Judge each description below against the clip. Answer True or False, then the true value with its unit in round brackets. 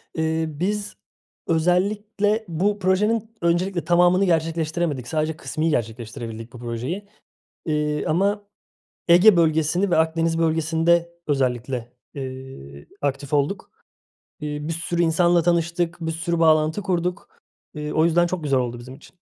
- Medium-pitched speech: True (165 Hz)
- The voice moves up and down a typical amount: True (3.1 semitones)